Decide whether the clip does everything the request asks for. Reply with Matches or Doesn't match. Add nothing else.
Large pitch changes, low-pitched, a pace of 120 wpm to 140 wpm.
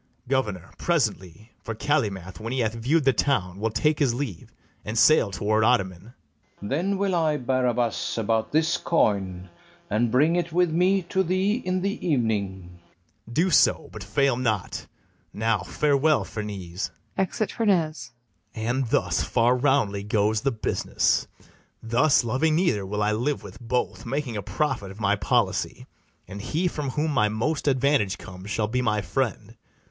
Doesn't match